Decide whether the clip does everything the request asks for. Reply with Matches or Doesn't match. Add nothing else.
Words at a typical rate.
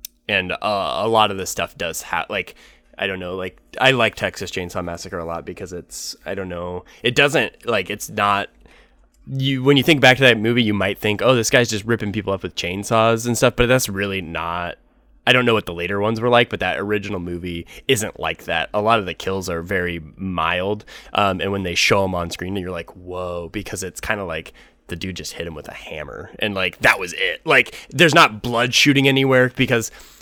Doesn't match